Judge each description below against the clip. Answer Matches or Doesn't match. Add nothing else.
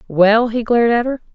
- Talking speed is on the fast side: Matches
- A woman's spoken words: Matches